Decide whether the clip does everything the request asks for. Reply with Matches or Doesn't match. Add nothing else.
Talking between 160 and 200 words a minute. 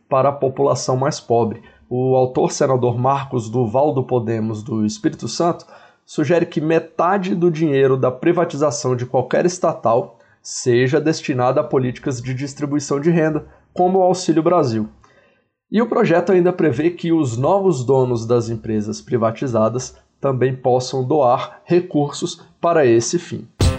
Doesn't match